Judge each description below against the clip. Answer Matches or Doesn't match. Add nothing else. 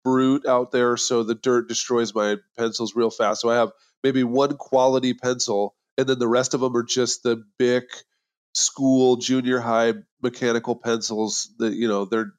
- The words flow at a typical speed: Matches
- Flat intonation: Matches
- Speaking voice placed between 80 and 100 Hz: Doesn't match